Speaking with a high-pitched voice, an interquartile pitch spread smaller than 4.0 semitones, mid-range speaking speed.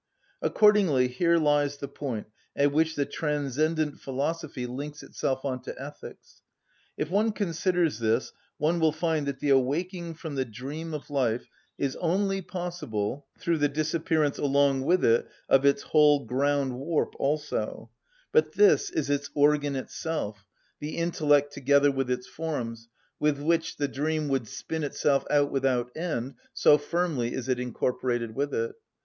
No: medium, 145 Hz; average, 3.4 semitones; average, 150 wpm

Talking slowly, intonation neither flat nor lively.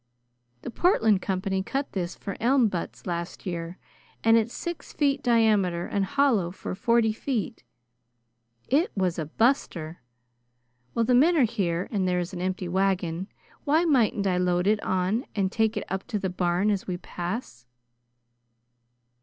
No: average, 160 wpm; average, 4.4 semitones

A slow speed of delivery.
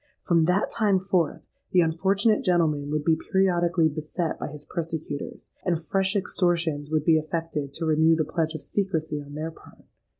No: average, 170 wpm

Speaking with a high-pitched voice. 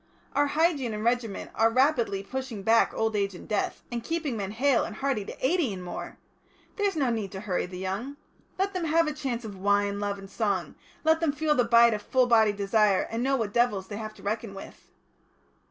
Yes: high, 230 Hz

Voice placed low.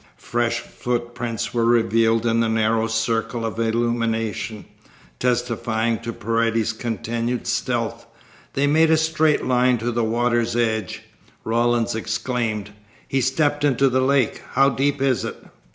Yes: low, 115 Hz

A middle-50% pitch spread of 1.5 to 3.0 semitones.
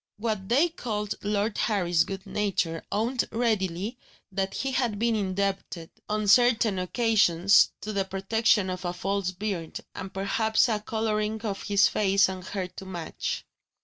Yes: narrow, 2.6 semitones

